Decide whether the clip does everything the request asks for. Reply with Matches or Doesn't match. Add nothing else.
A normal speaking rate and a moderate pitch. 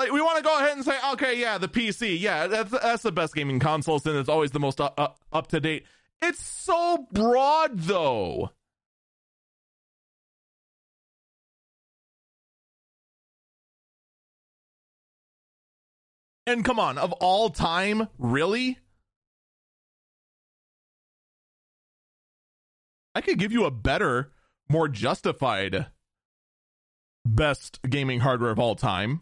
Doesn't match